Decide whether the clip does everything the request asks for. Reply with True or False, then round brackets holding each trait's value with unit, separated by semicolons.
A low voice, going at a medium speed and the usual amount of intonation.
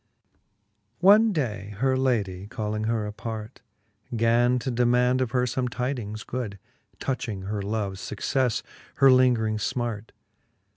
False (115 Hz; 125 wpm; 3.2 semitones)